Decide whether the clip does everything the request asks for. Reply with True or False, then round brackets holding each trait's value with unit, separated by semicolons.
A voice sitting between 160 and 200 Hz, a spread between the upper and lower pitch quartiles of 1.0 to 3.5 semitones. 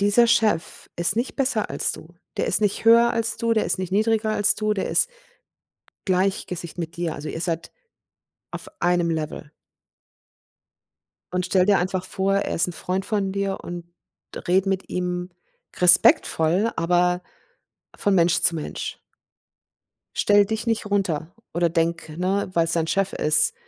True (185 Hz; 3.1 semitones)